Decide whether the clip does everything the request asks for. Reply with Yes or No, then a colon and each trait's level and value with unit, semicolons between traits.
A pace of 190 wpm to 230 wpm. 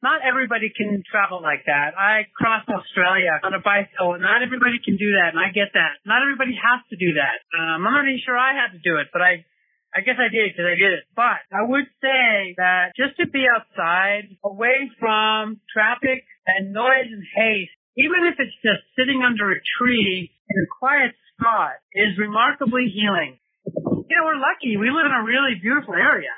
Yes: fast, 205 wpm